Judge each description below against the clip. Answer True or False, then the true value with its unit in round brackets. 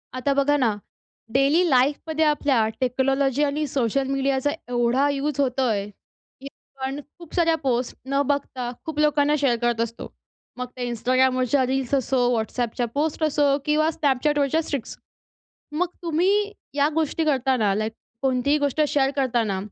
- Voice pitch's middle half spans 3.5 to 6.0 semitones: False (2.7 semitones)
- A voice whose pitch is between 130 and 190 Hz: False (275 Hz)